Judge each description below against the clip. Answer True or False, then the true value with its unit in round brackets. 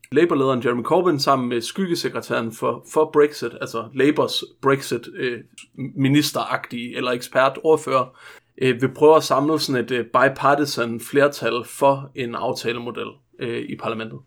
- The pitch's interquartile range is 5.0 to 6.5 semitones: False (3.5 semitones)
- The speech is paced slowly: True (130 wpm)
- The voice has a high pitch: False (135 Hz)